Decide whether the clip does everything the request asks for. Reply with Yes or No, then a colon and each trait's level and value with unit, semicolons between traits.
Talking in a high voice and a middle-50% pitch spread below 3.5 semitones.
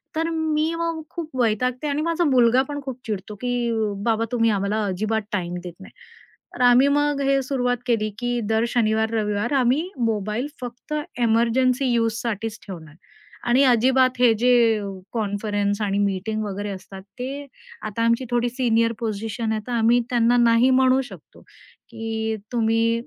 Yes: high, 230 Hz; average, 2.9 semitones